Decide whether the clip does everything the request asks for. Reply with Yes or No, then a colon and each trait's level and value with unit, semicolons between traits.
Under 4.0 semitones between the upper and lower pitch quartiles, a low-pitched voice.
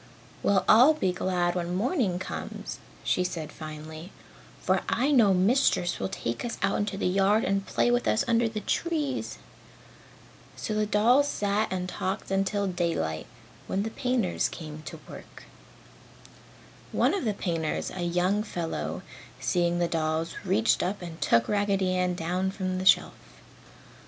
No: average, 3.4 semitones; high, 190 Hz